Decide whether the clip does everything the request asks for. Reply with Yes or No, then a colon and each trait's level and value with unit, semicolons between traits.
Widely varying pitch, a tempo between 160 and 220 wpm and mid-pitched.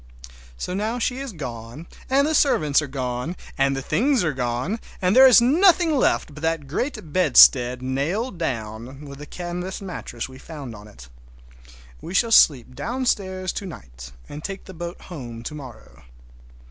Yes: wide, 7.7 semitones; average, 170 wpm; medium, 155 Hz